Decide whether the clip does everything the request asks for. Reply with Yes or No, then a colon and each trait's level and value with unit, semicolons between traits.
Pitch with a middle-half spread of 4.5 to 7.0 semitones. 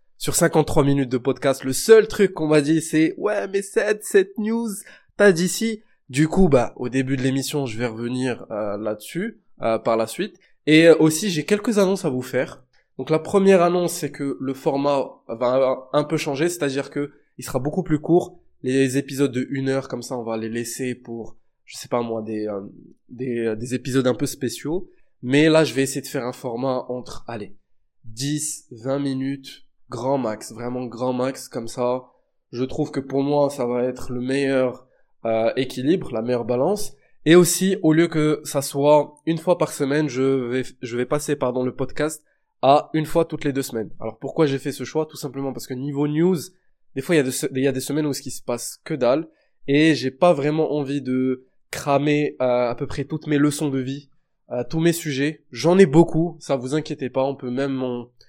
No: average, 3.6 semitones